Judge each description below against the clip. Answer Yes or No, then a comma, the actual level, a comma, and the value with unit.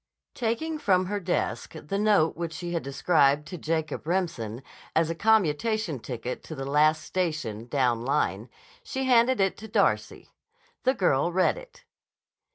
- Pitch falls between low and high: Yes, medium, 165 Hz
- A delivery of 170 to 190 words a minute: No, average, 155 wpm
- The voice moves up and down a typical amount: No, wide, 6.7 semitones